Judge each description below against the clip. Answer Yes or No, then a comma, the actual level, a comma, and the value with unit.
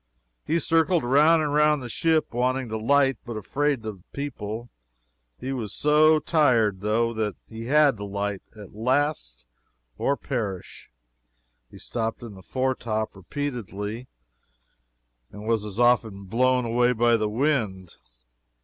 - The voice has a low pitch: Yes, low, 120 Hz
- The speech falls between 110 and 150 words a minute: Yes, average, 140 wpm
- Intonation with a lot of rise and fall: No, average, 4.9 semitones